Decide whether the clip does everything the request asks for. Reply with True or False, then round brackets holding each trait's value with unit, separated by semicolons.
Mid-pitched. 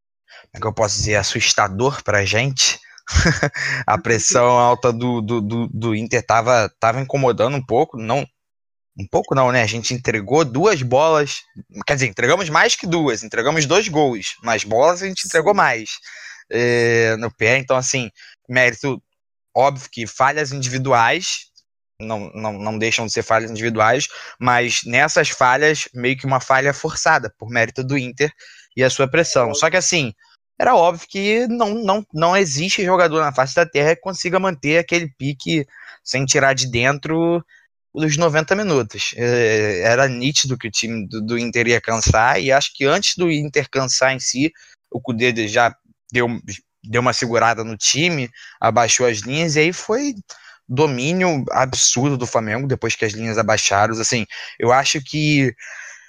False (130 Hz)